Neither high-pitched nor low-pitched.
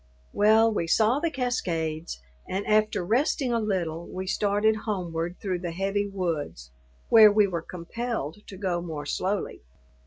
No: high, 195 Hz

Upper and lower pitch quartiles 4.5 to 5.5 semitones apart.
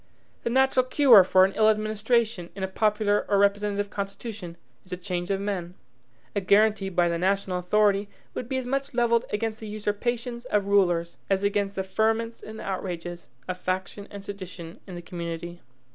No: average, 2.9 semitones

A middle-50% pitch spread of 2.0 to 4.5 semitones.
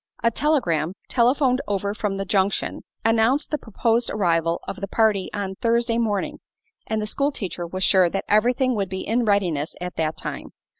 Yes: average, 3.8 semitones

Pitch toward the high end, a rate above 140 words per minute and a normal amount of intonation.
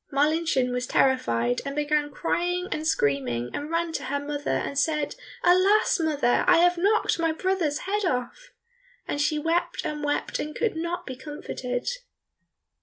Yes: very high, 300 Hz; average, 160 wpm; average, 4.0 semitones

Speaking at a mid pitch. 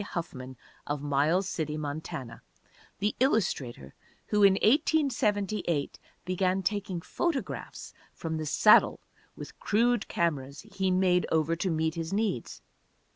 Yes: medium, 180 Hz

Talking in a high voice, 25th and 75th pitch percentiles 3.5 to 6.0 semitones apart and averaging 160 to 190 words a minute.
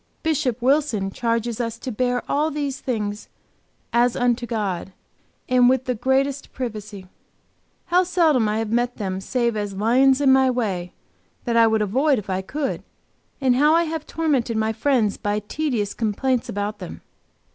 Yes: high, 240 Hz; average, 4.0 semitones; average, 165 wpm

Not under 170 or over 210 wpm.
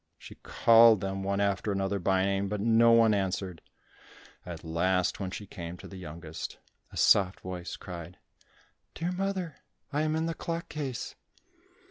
No: average, 160 wpm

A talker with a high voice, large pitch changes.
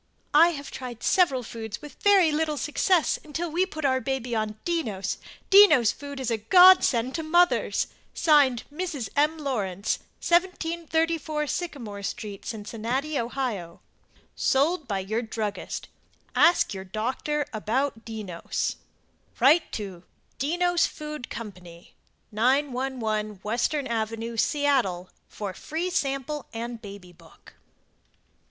Yes: very high, 260 Hz; wide, 6.0 semitones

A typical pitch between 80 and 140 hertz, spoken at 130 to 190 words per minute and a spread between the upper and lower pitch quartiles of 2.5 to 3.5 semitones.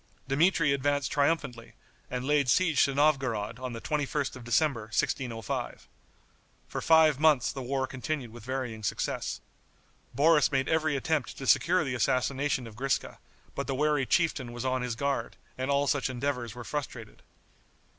Yes: low, 135 Hz; average, 155 wpm; average, 3.0 semitones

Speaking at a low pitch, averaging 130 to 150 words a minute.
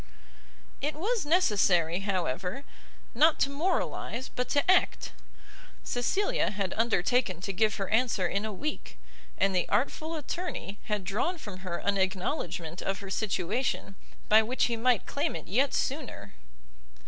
No: high, 215 Hz; average, 145 wpm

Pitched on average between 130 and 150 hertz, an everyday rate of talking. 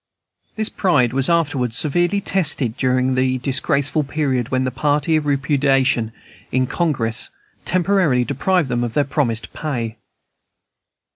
No: low, 135 Hz; slow, 130 wpm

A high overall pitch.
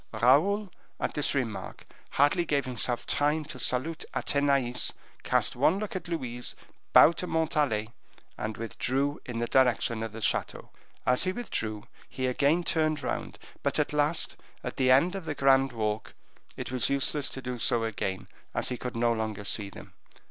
No: low, 130 Hz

